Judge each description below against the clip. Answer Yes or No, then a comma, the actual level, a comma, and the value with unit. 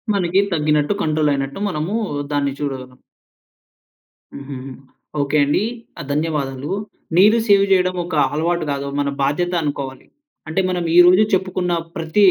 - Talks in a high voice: No, medium, 155 Hz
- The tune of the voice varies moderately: Yes, average, 4.3 semitones